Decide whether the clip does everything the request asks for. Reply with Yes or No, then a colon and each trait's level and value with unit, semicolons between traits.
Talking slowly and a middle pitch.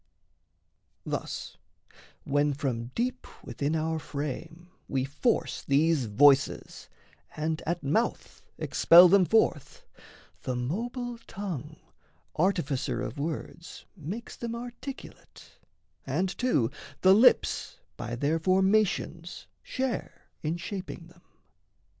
Yes: slow, 100 wpm; medium, 165 Hz